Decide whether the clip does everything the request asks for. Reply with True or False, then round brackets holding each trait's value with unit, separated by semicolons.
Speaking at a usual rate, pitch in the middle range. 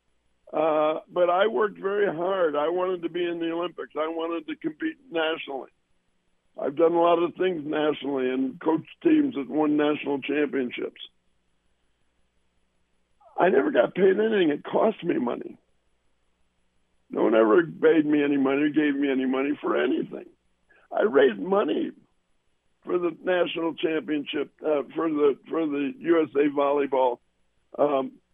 True (150 wpm; 145 Hz)